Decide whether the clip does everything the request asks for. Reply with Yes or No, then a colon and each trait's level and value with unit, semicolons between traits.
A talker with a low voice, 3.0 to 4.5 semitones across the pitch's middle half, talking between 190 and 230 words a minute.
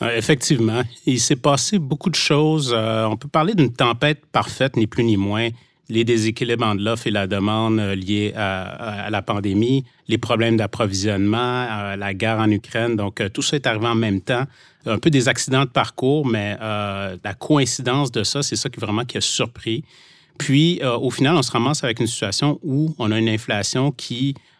Yes: low, 115 Hz; average, 4.2 semitones; average, 195 wpm